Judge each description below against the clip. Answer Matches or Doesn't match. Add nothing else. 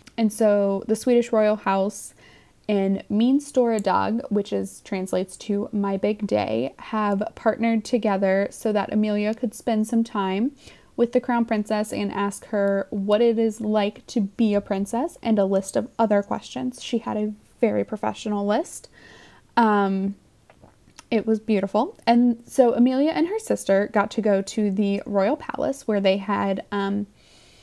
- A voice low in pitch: Doesn't match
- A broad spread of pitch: Doesn't match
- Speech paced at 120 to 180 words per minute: Matches